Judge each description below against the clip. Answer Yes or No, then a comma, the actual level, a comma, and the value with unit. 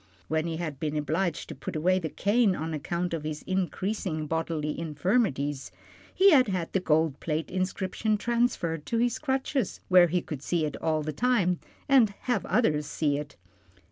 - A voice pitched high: No, medium, 170 Hz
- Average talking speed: Yes, average, 175 wpm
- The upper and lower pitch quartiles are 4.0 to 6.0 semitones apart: Yes, average, 4.9 semitones